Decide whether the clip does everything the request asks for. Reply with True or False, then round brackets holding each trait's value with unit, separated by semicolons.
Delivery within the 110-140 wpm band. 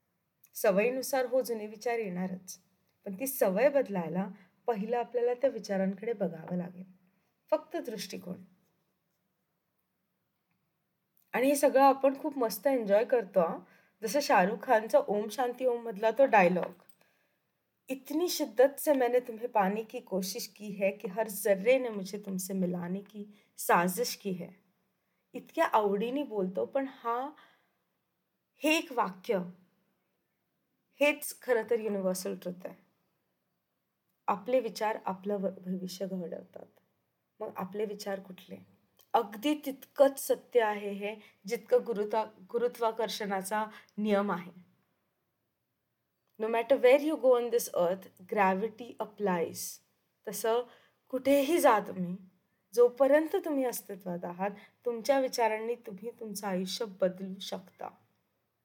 True (115 wpm)